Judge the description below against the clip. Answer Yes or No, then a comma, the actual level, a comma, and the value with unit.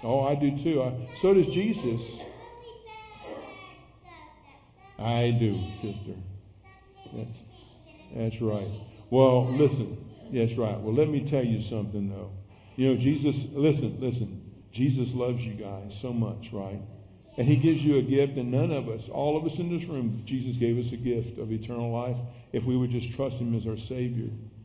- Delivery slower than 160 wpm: No, average, 175 wpm